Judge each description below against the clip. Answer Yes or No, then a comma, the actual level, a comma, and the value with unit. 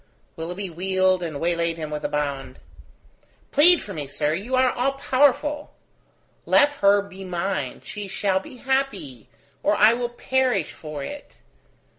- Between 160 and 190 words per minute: No, average, 150 wpm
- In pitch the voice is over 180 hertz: Yes, high, 190 Hz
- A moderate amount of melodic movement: No, wide, 7.9 semitones